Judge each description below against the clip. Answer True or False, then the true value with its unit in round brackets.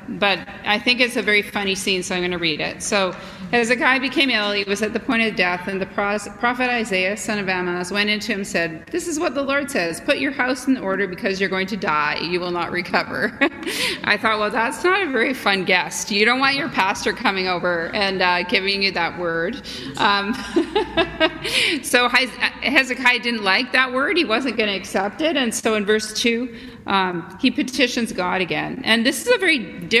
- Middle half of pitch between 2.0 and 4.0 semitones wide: False (5.1 semitones)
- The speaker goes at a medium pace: False (220 wpm)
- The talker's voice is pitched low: False (215 Hz)